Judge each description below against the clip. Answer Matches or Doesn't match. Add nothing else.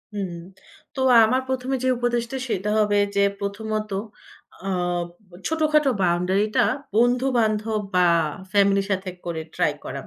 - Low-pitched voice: Doesn't match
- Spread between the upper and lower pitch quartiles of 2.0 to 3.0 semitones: Doesn't match